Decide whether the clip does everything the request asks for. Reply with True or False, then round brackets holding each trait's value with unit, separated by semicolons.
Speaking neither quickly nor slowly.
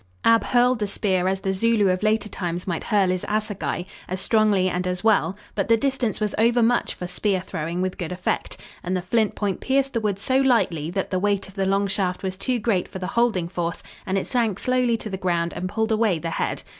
False (230 wpm)